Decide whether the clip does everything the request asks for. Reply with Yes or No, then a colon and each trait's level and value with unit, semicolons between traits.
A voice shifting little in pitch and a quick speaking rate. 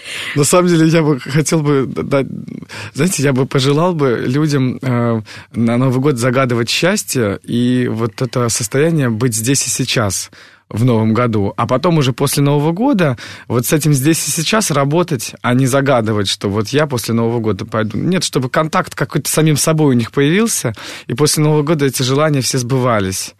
No: average, 4.2 semitones; fast, 175 wpm